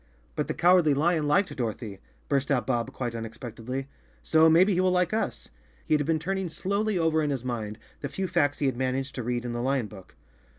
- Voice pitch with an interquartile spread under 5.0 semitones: No, wide, 5.4 semitones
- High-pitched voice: No, medium, 140 Hz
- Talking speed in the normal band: No, fast, 215 wpm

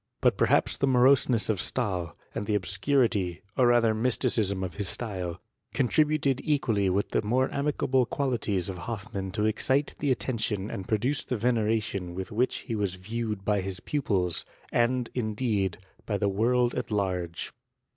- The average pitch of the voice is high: No, low, 110 Hz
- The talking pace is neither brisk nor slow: Yes, average, 160 wpm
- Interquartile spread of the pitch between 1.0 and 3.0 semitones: No, average, 4.5 semitones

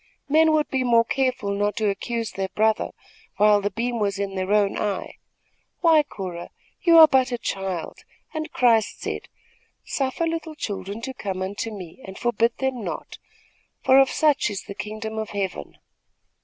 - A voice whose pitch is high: Yes, high, 220 Hz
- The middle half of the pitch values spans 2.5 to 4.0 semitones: No, average, 4.8 semitones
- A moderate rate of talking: Yes, average, 170 wpm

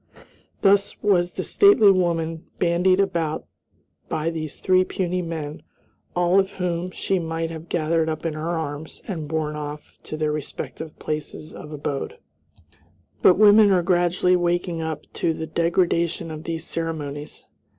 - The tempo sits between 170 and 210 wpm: No, average, 150 wpm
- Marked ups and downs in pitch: No, narrow, 2.4 semitones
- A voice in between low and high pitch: Yes, medium, 165 Hz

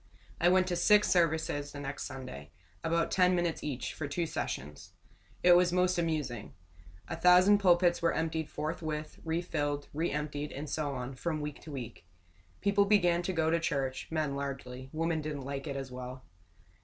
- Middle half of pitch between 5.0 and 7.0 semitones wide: No, average, 3.8 semitones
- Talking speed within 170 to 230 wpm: Yes, average, 175 wpm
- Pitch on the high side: No, medium, 155 Hz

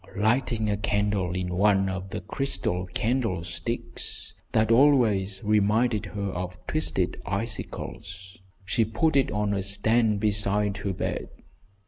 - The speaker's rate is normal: No, slow, 125 wpm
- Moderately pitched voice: No, low, 105 Hz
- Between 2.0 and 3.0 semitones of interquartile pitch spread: Yes, average, 2.7 semitones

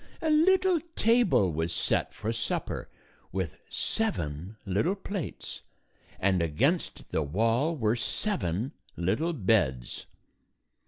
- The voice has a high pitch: No, low, 115 Hz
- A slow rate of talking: Yes, slow, 105 wpm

